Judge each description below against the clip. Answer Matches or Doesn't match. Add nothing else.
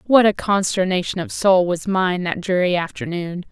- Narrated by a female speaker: Matches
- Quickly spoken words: Doesn't match